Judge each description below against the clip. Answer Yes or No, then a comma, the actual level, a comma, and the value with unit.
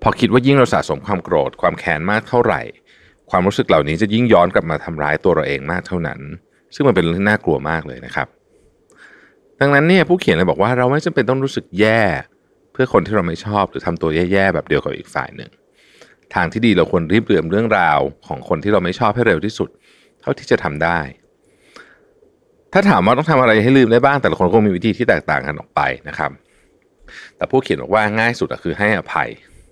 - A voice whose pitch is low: Yes, low, 120 Hz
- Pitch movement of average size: No, wide, 8.1 semitones